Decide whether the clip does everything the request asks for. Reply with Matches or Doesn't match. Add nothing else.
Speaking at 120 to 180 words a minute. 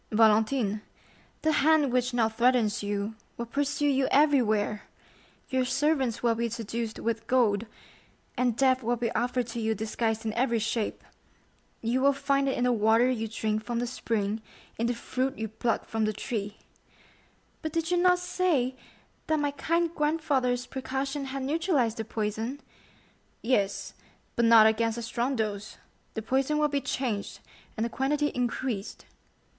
Matches